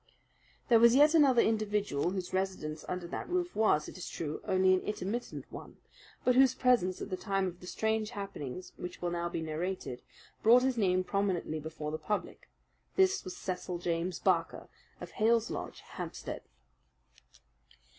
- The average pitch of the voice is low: No, high, 190 Hz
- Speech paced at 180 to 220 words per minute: No, average, 165 wpm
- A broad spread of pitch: No, average, 4.4 semitones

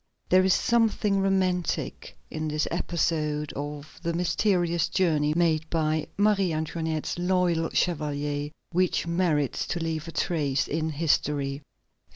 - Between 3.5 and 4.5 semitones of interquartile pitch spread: No, average, 2.9 semitones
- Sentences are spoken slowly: Yes, slow, 125 wpm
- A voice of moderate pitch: Yes, medium, 165 Hz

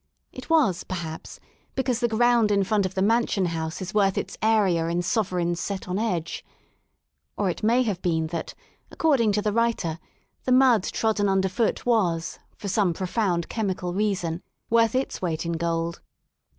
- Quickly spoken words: No, average, 165 wpm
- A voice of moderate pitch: No, high, 195 Hz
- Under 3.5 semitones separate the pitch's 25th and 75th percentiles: No, average, 4.5 semitones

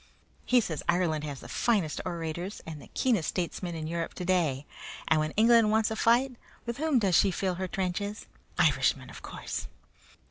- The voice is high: No, medium, 180 Hz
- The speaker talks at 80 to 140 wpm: No, average, 175 wpm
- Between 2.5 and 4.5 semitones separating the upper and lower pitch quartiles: No, wide, 5.5 semitones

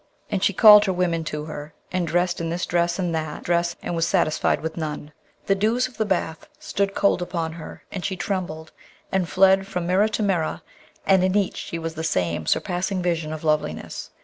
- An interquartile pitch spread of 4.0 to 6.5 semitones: No, average, 3.1 semitones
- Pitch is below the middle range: No, medium, 175 Hz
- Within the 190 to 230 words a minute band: Yes, fast, 205 wpm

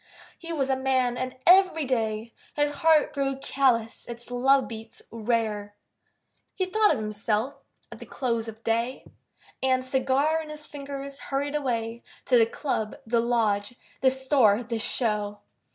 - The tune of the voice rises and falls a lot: No, average, 3.6 semitones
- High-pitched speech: Yes, very high, 255 Hz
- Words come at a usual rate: Yes, average, 150 wpm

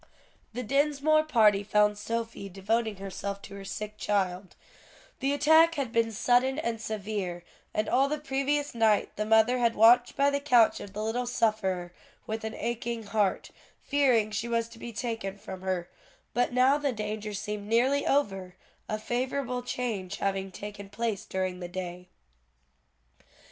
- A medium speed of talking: Yes, average, 160 wpm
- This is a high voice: Yes, high, 220 Hz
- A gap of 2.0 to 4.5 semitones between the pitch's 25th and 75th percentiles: Yes, average, 3.7 semitones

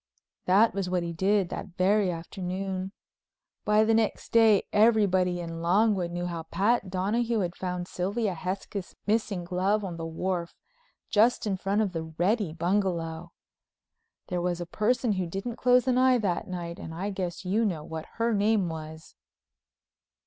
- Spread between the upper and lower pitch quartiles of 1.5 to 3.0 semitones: No, average, 3.4 semitones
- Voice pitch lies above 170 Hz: Yes, high, 190 Hz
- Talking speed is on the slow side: No, average, 165 wpm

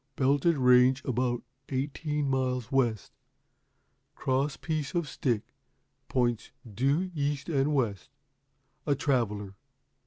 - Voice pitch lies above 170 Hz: No, low, 135 Hz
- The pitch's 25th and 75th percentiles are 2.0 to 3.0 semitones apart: Yes, average, 2.7 semitones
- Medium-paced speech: No, slow, 100 wpm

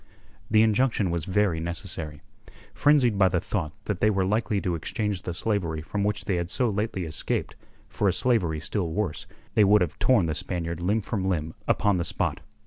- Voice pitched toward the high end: No, very low, 95 Hz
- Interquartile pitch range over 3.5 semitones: Yes, average, 3.9 semitones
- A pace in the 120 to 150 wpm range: No, average, 195 wpm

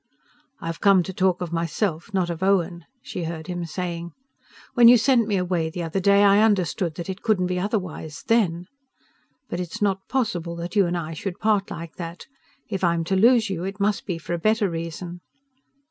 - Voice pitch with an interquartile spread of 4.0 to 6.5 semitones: No, average, 2.9 semitones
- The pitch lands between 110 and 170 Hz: No, medium, 180 Hz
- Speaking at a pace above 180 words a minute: Yes, average, 200 wpm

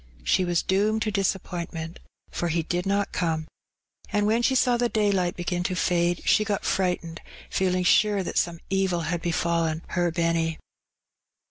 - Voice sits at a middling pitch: Yes, medium, 180 Hz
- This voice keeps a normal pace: Yes, average, 160 wpm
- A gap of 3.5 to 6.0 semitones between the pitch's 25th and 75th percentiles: No, average, 2.7 semitones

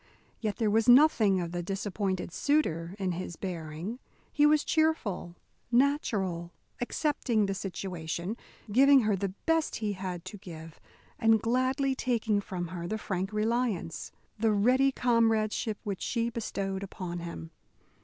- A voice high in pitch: Yes, high, 205 Hz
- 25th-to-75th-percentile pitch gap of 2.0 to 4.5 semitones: No, average, 4.9 semitones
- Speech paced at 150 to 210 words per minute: No, average, 140 wpm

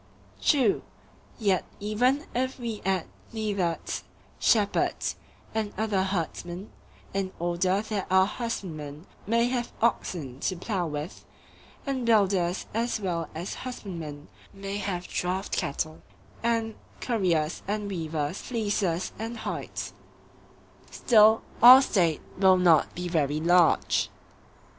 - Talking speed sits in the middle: No, slow, 110 wpm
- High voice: Yes, high, 195 Hz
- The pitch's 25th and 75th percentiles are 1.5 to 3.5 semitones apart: No, average, 4.4 semitones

